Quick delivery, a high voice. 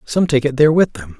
No: fast, 300 wpm; medium, 140 Hz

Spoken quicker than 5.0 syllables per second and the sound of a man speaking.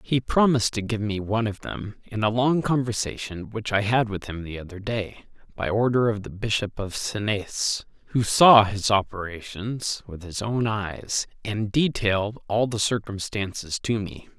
No: 4.5 syllables/s; male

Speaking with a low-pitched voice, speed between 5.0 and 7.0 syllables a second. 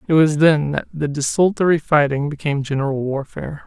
No: medium, 150 Hz; 5.5 syllables/s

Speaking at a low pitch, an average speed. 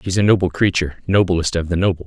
No: very low, 90 Hz; fast, 230 wpm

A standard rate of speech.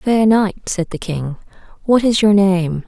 Yes: average, 190 wpm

